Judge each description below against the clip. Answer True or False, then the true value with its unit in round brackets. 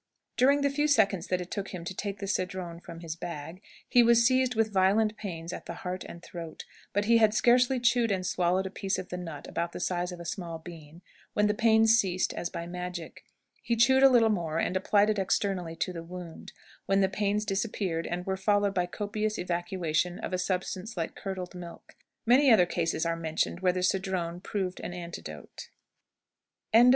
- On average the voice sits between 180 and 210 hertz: True (185 Hz)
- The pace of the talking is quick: True (210 wpm)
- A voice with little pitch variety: False (3.5 semitones)